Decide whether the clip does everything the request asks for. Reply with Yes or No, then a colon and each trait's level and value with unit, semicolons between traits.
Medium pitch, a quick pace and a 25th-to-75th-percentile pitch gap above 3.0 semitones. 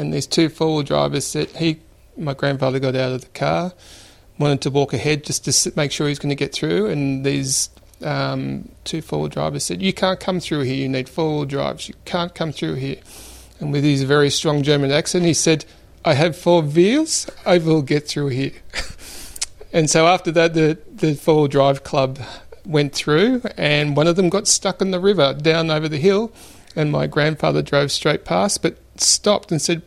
Yes: medium, 150 Hz; fast, 205 wpm; average, 3.4 semitones